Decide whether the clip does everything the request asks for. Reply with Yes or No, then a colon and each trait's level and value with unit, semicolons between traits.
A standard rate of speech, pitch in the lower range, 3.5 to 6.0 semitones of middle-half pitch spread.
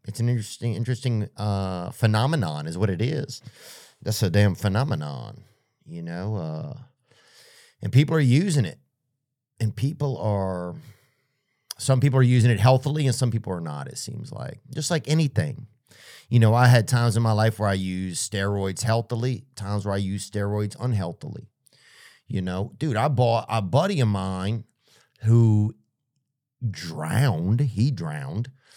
Yes: average, 155 wpm; low, 120 Hz; average, 4.3 semitones